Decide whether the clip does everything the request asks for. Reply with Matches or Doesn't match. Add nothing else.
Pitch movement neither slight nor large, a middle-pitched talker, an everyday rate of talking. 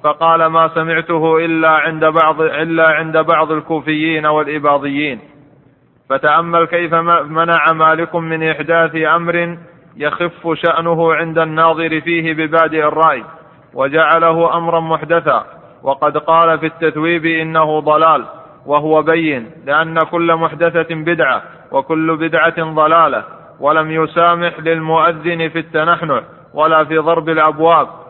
Doesn't match